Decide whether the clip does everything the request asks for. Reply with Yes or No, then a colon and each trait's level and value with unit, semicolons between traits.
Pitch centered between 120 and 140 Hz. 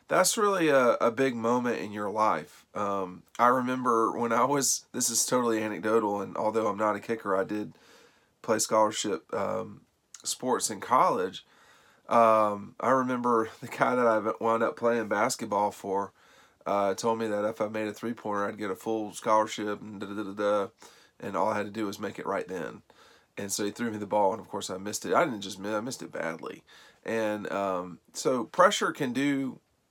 No: low, 110 Hz